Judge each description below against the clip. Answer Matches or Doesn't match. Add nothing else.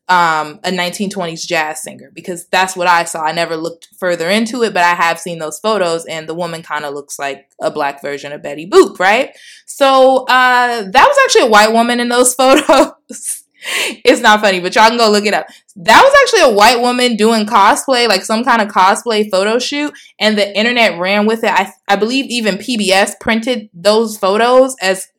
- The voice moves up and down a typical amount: Doesn't match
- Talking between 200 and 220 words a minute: Matches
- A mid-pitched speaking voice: Doesn't match